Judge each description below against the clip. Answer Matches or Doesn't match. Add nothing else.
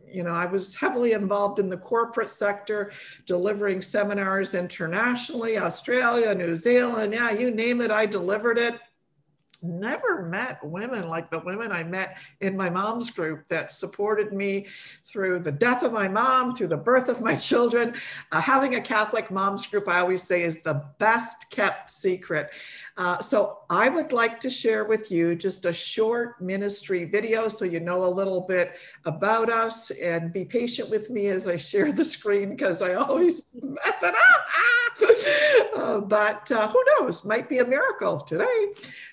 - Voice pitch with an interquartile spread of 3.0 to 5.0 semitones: Matches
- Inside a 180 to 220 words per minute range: Doesn't match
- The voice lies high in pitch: Matches